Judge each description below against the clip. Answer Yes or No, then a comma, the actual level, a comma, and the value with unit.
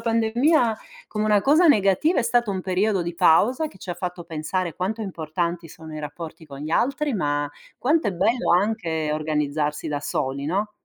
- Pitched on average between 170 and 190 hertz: Yes, medium, 185 Hz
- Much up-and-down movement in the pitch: Yes, wide, 5.9 semitones